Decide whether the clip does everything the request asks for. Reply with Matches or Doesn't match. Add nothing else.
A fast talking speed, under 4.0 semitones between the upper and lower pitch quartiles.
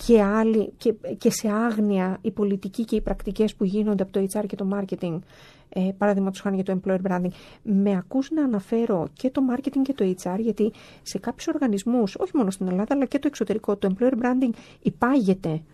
Matches